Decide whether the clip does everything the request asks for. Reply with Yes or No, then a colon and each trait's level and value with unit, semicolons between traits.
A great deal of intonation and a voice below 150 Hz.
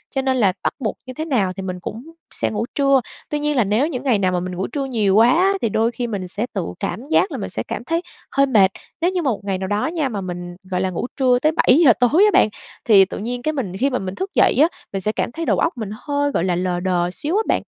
No: wide, 6.6 semitones; high, 235 Hz